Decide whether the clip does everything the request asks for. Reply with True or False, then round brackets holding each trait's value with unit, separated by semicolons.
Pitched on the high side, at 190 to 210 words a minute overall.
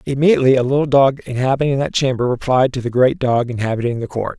False (130 Hz; 205 wpm)